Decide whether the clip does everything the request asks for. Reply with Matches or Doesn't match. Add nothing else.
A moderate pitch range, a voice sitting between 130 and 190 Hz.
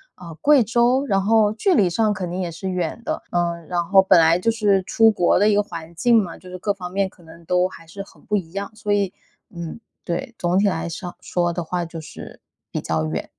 Matches